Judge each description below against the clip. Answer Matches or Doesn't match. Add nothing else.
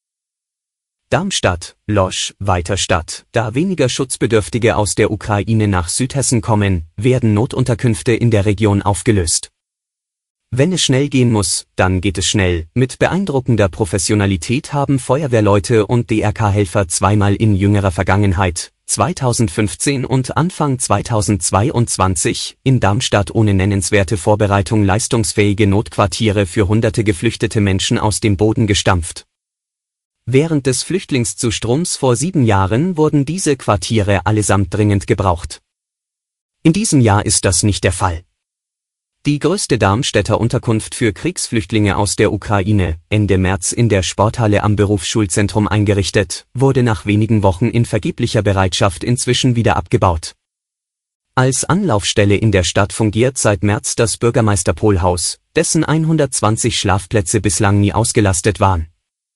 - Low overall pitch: Matches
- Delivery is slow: Matches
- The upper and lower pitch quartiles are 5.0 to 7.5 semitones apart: Doesn't match